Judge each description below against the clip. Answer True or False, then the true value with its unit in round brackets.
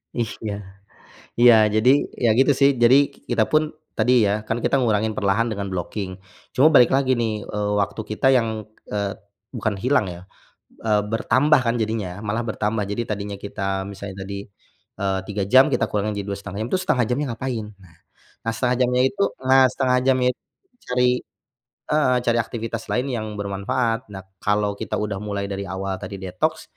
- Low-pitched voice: True (110 Hz)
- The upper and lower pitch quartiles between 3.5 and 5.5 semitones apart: True (3.8 semitones)